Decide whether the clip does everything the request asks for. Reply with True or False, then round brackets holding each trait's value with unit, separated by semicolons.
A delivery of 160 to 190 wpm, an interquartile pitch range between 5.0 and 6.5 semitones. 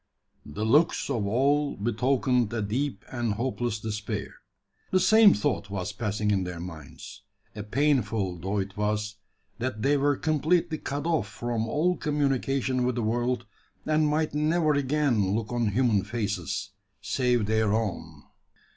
False (145 wpm; 5.3 semitones)